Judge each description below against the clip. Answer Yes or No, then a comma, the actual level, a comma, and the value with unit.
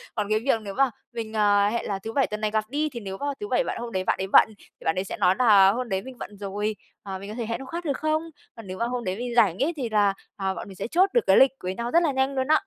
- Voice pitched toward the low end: No, high, 220 Hz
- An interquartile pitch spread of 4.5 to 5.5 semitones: Yes, average, 4.9 semitones